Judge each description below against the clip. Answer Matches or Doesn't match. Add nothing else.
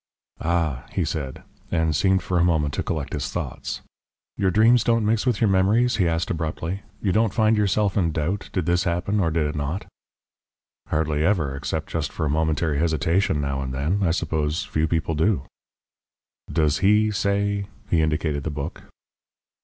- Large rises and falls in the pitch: Doesn't match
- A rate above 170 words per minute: Matches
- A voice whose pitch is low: Matches